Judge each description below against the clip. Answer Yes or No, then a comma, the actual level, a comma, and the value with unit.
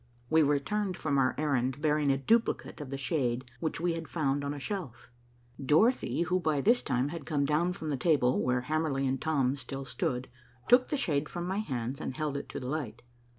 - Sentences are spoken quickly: Yes, fast, 210 wpm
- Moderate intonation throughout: Yes, average, 3.6 semitones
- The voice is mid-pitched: Yes, medium, 145 Hz